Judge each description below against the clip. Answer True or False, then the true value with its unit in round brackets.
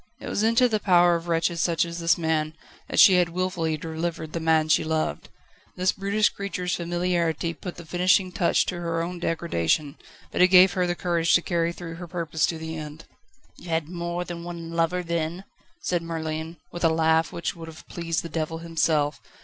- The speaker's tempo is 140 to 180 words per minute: False (200 wpm)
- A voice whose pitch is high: False (170 Hz)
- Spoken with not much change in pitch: True (1.6 semitones)